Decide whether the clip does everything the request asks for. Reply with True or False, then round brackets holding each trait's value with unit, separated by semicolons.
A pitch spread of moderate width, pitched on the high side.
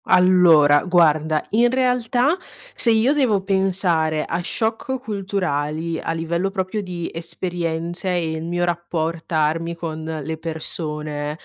False (3.4 semitones; 170 Hz)